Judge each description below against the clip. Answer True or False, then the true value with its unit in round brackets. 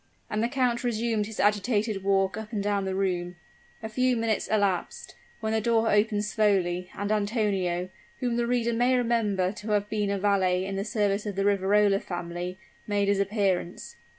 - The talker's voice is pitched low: False (205 Hz)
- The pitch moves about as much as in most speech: False (2.3 semitones)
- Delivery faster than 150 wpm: True (180 wpm)